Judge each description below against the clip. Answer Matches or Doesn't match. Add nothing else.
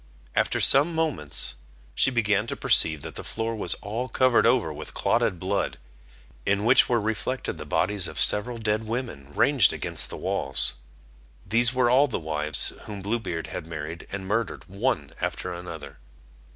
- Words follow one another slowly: Doesn't match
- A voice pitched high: Doesn't match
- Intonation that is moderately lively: Doesn't match